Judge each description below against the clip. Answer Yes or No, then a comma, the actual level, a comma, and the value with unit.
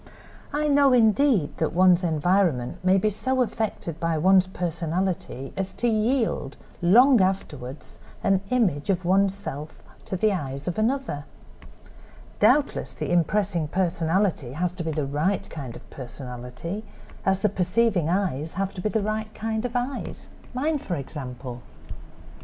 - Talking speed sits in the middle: Yes, average, 145 wpm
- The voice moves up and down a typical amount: No, wide, 5.7 semitones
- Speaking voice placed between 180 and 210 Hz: Yes, medium, 185 Hz